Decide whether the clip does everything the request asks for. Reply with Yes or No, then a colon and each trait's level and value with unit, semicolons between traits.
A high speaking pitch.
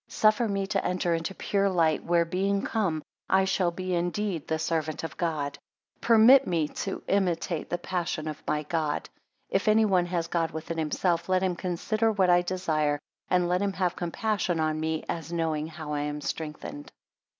No: medium, 175 Hz